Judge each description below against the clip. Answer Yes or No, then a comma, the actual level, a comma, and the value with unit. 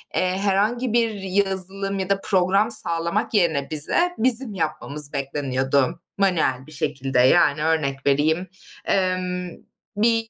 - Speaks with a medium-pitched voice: Yes, medium, 180 Hz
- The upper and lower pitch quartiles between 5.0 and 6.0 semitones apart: Yes, average, 5.3 semitones